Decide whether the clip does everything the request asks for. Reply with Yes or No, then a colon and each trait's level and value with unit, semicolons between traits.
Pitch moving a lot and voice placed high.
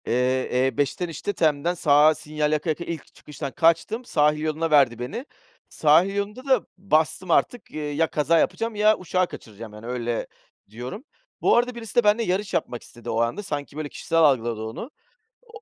No: wide, 6.3 semitones; medium, 155 Hz